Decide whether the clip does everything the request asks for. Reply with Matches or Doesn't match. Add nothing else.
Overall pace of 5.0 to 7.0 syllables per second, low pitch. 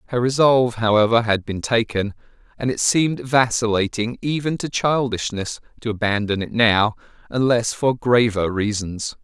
Doesn't match